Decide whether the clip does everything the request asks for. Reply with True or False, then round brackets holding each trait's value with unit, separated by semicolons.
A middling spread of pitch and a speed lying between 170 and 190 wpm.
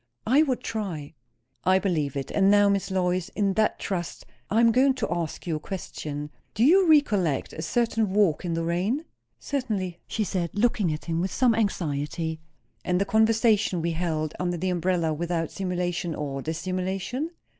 True (4.6 semitones; 175 wpm)